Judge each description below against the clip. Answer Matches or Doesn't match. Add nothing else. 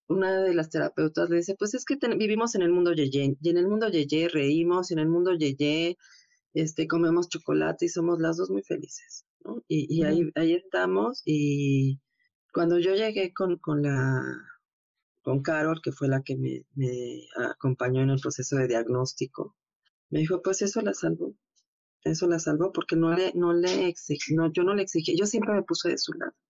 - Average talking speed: Doesn't match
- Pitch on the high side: Doesn't match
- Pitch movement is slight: Doesn't match